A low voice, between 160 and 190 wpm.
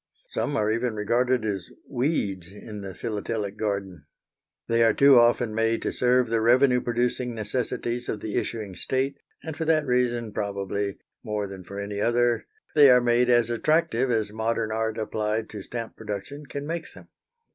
Yes: low, 115 Hz; average, 170 wpm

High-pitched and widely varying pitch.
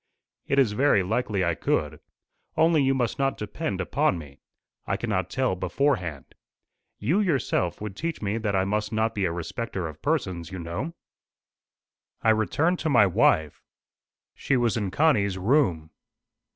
No: low, 105 Hz; wide, 6.7 semitones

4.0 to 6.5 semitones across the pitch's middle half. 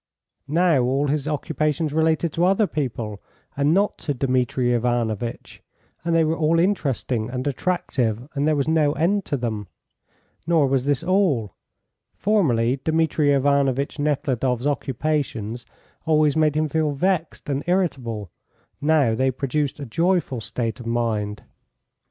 Yes: average, 4.4 semitones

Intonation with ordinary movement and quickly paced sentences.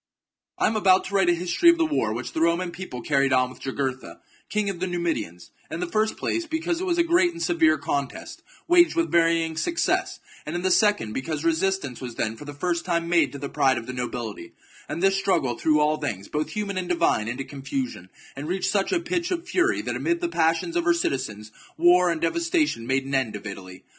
No: wide, 7.8 semitones; fast, 230 wpm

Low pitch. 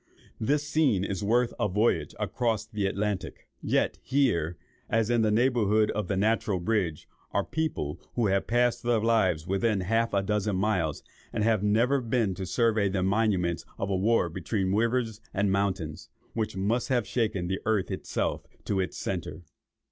Yes: low, 105 Hz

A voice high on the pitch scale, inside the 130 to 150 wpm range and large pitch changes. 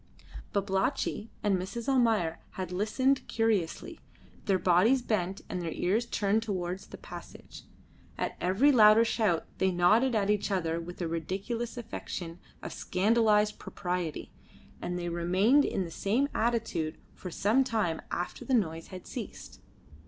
No: high, 200 Hz; average, 145 wpm; average, 4.3 semitones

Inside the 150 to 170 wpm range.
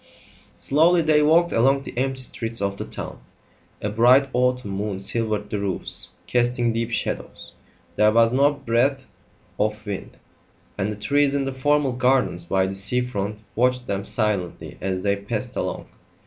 Yes: average, 160 wpm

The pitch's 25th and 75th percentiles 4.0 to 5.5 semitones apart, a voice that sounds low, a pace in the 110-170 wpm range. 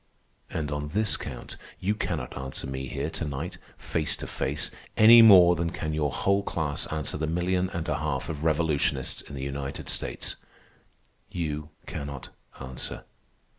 No: average, 3.6 semitones; very low, 75 Hz; average, 160 wpm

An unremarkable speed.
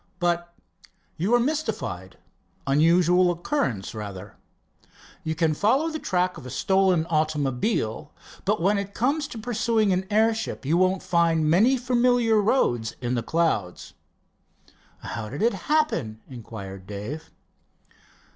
No: slow, 130 wpm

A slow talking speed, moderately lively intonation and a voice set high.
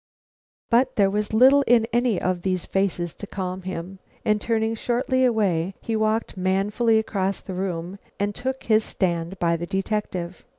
No: average, 165 wpm; average, 3.4 semitones; high, 200 Hz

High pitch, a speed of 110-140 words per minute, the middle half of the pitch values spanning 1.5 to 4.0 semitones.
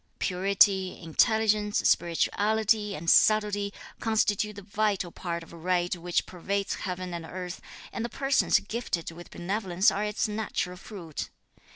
Yes: high, 195 Hz; slow, 135 wpm; average, 3.1 semitones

